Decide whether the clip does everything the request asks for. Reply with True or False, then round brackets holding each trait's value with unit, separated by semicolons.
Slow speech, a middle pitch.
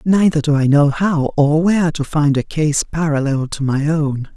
False (205 wpm; 150 Hz)